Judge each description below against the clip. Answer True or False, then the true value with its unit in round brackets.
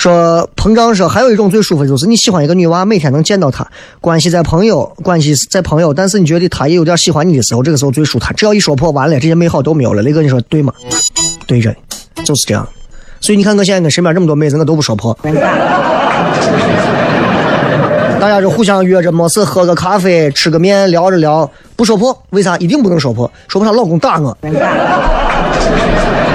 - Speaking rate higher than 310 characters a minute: True (330 characters per minute)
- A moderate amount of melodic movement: True (4.3 semitones)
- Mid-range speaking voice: True (170 Hz)